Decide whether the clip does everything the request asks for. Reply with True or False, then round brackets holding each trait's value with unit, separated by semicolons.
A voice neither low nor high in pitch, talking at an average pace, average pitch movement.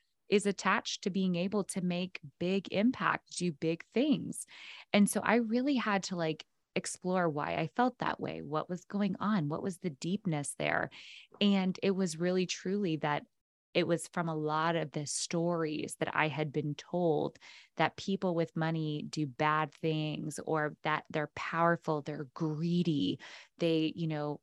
True (170 Hz; 170 wpm; 3.6 semitones)